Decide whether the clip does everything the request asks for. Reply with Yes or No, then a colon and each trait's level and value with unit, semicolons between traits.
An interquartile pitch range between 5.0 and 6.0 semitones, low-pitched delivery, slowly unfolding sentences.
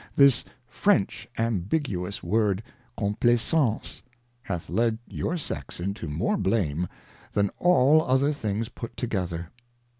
Yes: wide, 5.6 semitones; low, 110 Hz; slow, 110 wpm